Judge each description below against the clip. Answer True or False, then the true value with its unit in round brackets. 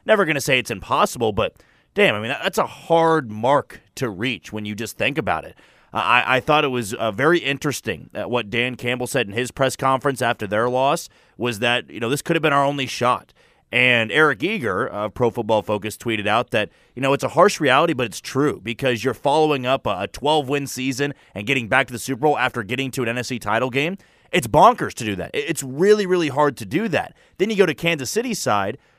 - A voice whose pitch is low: True (130 Hz)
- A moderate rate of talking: False (240 wpm)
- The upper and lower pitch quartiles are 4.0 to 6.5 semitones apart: False (3.4 semitones)